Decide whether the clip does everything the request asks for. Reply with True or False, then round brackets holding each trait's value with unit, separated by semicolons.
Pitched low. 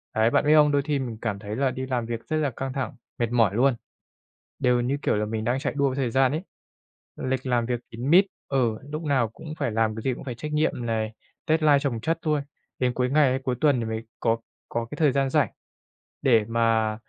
True (125 Hz)